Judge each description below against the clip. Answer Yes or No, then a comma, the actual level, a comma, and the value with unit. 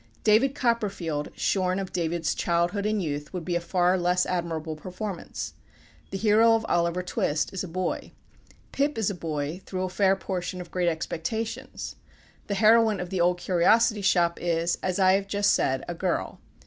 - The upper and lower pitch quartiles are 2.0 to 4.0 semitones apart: Yes, average, 2.9 semitones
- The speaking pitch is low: No, medium, 180 Hz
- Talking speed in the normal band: Yes, average, 175 wpm